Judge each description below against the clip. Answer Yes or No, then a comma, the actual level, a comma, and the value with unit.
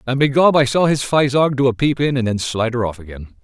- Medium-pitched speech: No, low, 130 Hz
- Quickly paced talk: Yes, fast, 260 wpm